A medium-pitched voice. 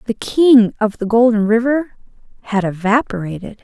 No: high, 225 Hz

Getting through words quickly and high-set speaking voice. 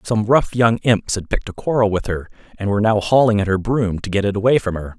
No: fast, 275 wpm; low, 105 Hz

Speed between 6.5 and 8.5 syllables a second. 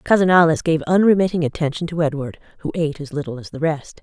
Yes: 6.7 syllables/s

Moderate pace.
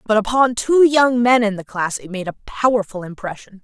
No: fast, 215 wpm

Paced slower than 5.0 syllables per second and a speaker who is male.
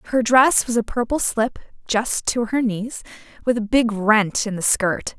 No: 4.0 syllables/s; female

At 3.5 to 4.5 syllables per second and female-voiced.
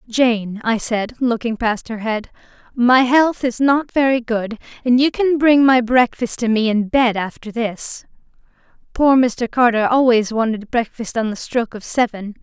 Yes: 4.4 syllables/s; female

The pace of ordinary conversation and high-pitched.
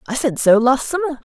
No: fast, 230 wpm; very high, 270 Hz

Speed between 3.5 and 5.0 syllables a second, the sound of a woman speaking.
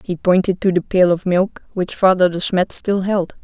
Yes: 4.7 syllables/s; female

